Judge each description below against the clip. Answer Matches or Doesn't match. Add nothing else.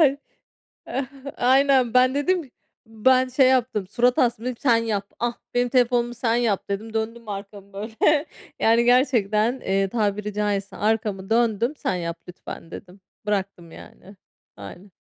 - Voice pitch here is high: Matches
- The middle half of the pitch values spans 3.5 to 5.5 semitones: Matches